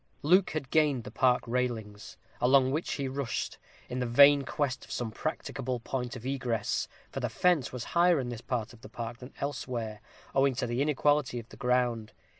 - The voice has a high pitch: No, low, 125 Hz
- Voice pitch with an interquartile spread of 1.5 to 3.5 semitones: Yes, average, 2.8 semitones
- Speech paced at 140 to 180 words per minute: No, average, 195 wpm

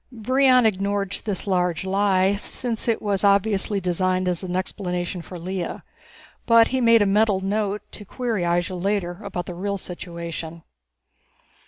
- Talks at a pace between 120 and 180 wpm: Yes, average, 150 wpm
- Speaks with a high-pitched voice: Yes, high, 195 Hz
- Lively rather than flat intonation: No, average, 2.8 semitones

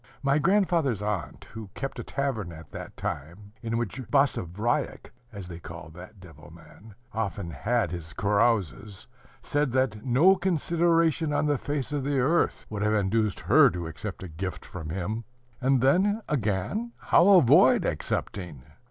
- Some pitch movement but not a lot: No, wide, 7.4 semitones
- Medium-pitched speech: No, low, 110 Hz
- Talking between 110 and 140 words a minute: No, average, 155 wpm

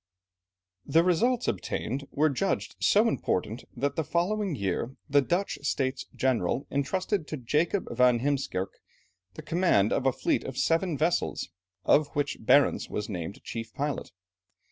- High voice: No, medium, 140 Hz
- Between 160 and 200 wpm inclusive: No, average, 145 wpm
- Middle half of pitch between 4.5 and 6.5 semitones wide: Yes, wide, 5.4 semitones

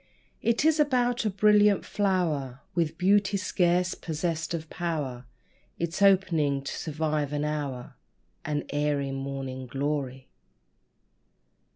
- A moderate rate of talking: No, slow, 110 wpm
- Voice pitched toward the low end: No, medium, 155 Hz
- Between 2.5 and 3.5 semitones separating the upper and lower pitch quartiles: No, wide, 5.5 semitones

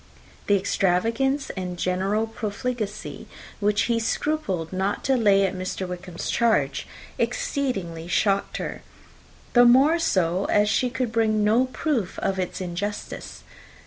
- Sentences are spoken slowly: Yes, slow, 130 wpm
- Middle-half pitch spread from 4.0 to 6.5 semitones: Yes, average, 4.4 semitones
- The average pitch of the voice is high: Yes, high, 205 Hz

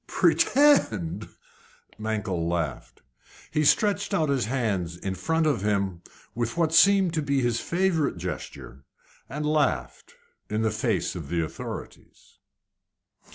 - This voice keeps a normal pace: No, slow, 125 wpm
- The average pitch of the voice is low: Yes, low, 120 Hz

